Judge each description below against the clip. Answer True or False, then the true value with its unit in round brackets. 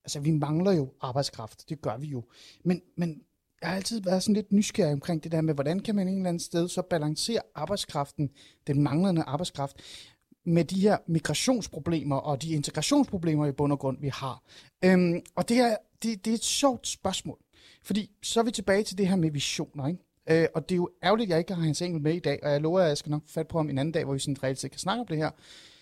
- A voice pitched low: False (160 Hz)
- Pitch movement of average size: True (4.3 semitones)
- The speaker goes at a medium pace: False (250 wpm)